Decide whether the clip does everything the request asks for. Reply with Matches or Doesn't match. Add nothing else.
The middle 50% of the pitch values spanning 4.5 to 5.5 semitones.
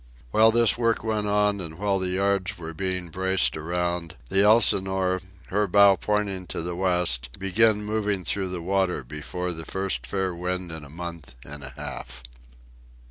Doesn't match